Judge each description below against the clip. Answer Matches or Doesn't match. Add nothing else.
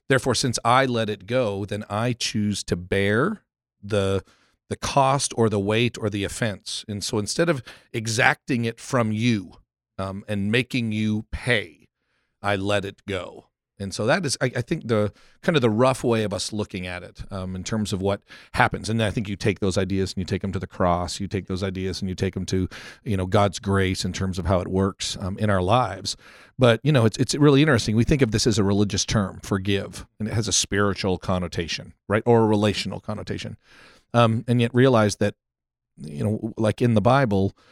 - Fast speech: Matches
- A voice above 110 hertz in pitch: Doesn't match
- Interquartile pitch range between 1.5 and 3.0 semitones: Doesn't match